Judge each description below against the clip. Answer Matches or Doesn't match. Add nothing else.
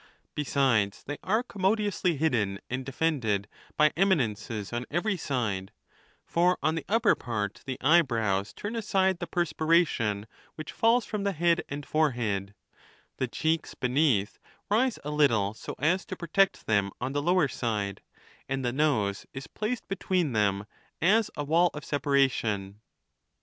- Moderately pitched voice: Matches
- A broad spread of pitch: Matches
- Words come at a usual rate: Matches